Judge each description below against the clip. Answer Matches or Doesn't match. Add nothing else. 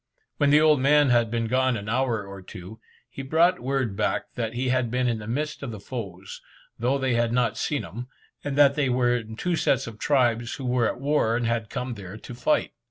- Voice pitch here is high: Doesn't match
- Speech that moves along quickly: Matches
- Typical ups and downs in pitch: Matches